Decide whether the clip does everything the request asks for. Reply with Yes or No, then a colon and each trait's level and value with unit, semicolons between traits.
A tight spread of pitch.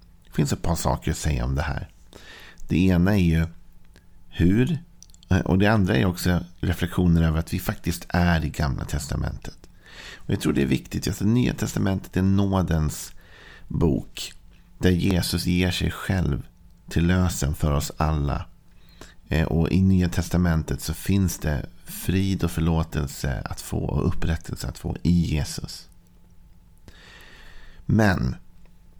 Yes: narrow, 2.0 semitones